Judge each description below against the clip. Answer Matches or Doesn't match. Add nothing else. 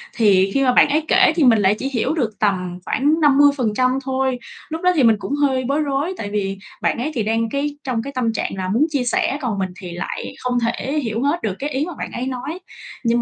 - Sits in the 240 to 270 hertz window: Matches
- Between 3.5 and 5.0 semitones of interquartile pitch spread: Matches